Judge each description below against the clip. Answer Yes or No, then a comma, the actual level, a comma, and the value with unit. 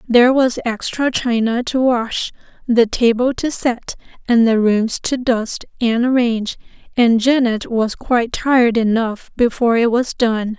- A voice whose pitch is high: Yes, high, 235 Hz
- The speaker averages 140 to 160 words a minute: Yes, average, 155 wpm